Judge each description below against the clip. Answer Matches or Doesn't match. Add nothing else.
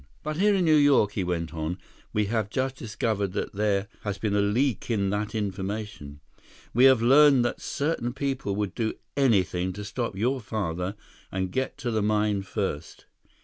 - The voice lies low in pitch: Matches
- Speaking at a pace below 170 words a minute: Doesn't match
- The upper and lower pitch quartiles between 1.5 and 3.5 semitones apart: Doesn't match